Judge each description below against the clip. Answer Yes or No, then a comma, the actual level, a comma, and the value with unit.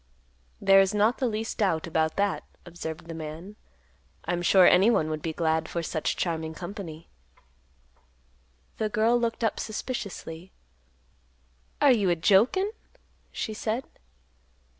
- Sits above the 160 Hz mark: Yes, high, 190 Hz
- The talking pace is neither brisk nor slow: No, slow, 130 wpm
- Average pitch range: Yes, average, 5.0 semitones